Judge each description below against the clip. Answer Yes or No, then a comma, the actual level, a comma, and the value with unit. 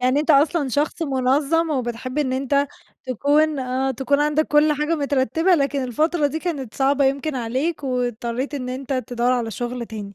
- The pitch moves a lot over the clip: No, average, 2.9 semitones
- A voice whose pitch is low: No, very high, 275 Hz